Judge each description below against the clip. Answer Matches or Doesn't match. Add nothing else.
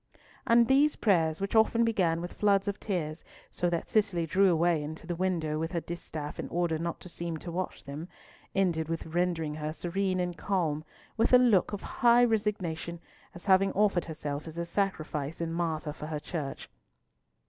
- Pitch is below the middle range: Doesn't match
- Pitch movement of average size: Matches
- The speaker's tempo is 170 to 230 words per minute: Matches